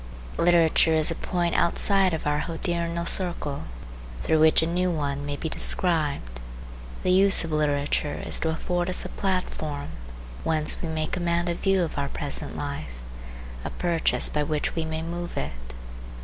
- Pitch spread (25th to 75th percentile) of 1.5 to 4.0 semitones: Yes, average, 2.9 semitones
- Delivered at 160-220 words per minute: Yes, average, 165 wpm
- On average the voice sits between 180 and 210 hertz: No, medium, 160 Hz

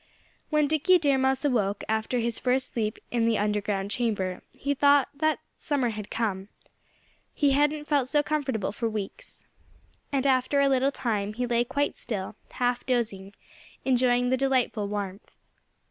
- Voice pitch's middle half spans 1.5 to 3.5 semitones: No, average, 4.7 semitones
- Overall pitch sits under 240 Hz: No, high, 245 Hz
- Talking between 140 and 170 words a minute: Yes, average, 155 wpm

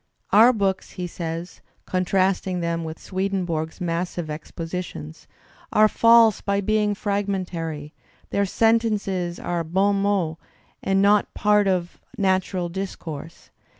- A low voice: No, medium, 185 Hz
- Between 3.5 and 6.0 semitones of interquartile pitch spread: No, average, 3.1 semitones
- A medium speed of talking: No, slow, 115 wpm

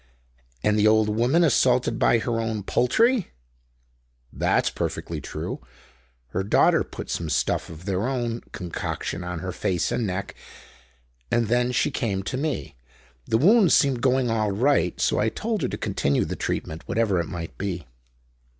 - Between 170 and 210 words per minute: No, average, 160 wpm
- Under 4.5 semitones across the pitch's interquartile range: No, average, 5.1 semitones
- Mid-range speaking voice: No, low, 115 Hz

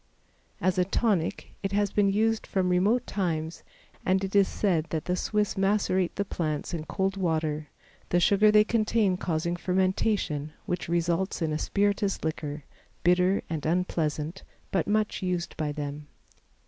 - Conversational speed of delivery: Yes, average, 155 wpm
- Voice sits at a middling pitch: Yes, medium, 180 Hz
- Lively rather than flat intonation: No, average, 3.8 semitones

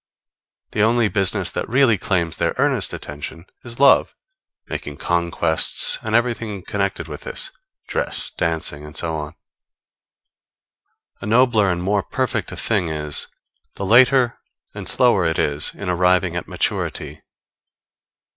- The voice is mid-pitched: No, very low, 95 Hz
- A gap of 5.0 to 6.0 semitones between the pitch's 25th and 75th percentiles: Yes, average, 5.3 semitones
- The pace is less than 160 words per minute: Yes, slow, 135 wpm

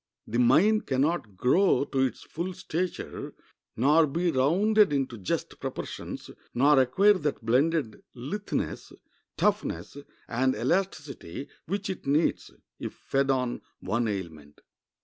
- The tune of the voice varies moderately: No, wide, 6.2 semitones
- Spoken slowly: Yes, slow, 125 wpm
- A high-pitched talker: No, medium, 140 Hz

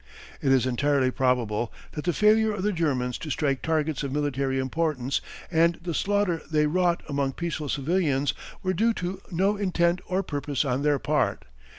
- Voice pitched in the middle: Yes, medium, 150 Hz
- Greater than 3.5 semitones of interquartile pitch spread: Yes, average, 4.6 semitones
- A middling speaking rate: Yes, average, 175 wpm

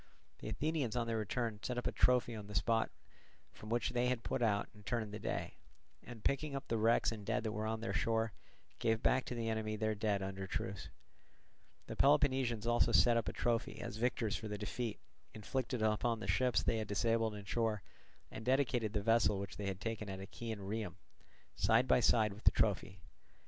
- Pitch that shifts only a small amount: Yes, narrow, 2.3 semitones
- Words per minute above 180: Yes, fast, 205 wpm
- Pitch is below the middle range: Yes, low, 110 Hz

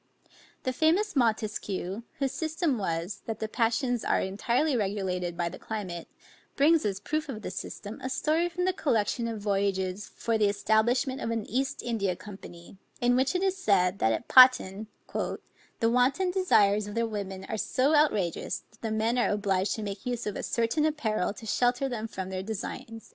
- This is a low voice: No, high, 220 Hz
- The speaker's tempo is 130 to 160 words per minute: No, average, 185 wpm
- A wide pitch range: No, average, 4.6 semitones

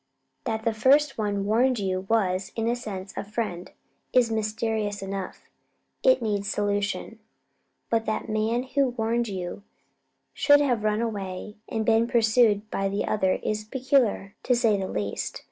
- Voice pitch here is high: Yes, high, 215 Hz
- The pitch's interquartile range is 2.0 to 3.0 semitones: Yes, average, 2.7 semitones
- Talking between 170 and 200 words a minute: No, average, 160 wpm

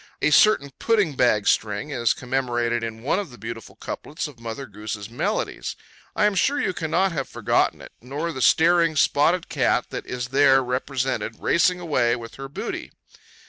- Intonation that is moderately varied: No, wide, 5.8 semitones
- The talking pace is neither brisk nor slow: Yes, average, 175 wpm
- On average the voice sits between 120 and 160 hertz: Yes, low, 135 Hz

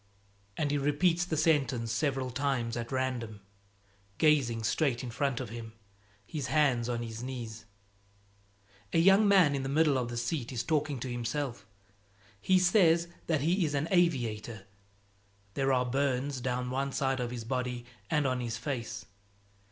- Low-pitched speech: Yes, low, 130 Hz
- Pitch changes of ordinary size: Yes, average, 3.9 semitones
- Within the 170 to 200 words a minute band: No, average, 160 wpm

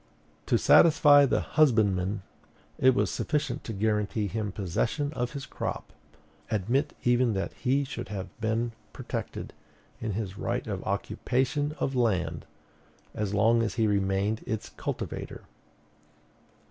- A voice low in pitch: Yes, low, 110 Hz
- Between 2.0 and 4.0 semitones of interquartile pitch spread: No, average, 4.5 semitones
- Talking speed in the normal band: No, slow, 130 wpm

